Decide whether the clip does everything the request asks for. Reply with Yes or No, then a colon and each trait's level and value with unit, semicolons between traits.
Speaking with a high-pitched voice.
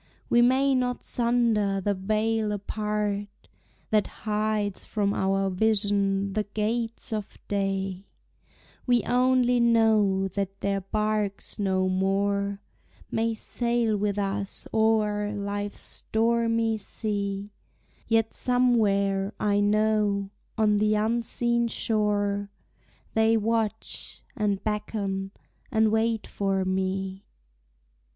Yes: high, 210 Hz